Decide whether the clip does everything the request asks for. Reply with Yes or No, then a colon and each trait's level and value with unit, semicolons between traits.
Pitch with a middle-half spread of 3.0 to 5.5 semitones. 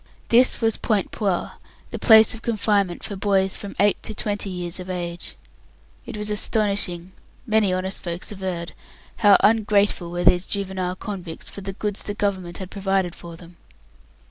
No: narrow, 2.6 semitones